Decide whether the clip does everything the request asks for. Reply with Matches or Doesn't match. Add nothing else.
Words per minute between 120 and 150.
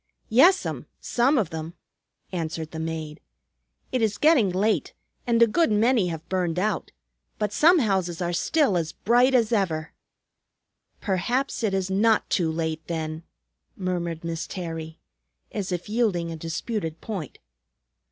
Matches